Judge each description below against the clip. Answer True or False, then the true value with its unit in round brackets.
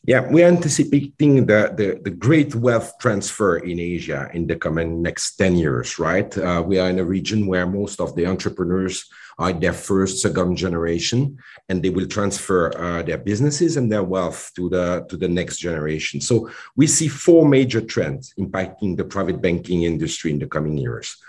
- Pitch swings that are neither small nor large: False (5.8 semitones)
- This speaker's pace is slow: False (185 wpm)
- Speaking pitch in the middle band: False (95 Hz)